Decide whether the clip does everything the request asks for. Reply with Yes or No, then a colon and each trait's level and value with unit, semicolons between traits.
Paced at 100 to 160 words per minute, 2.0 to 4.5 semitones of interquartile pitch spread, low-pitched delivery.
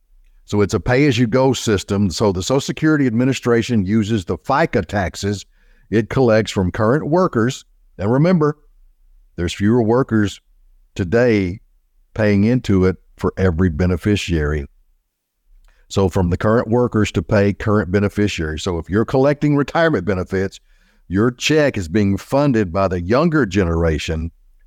No: slow, 135 wpm; average, 5.0 semitones; low, 105 Hz